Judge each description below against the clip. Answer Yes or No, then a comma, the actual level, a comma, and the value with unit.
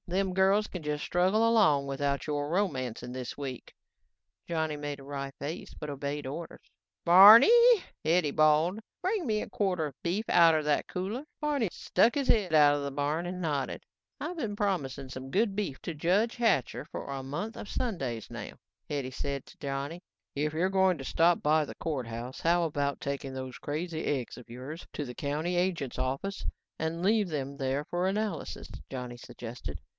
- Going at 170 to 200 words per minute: Yes, average, 180 wpm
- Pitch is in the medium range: Yes, medium, 155 Hz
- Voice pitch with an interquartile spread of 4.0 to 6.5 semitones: Yes, wide, 5.4 semitones